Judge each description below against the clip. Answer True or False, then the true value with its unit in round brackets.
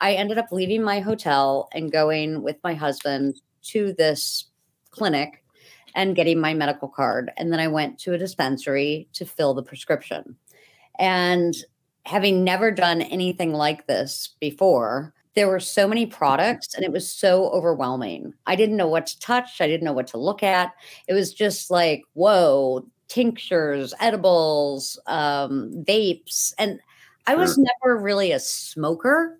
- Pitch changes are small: False (5.0 semitones)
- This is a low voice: False (170 Hz)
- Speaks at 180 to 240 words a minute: False (155 wpm)